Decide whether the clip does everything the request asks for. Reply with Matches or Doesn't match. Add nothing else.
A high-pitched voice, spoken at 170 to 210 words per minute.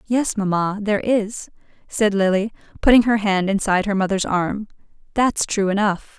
Doesn't match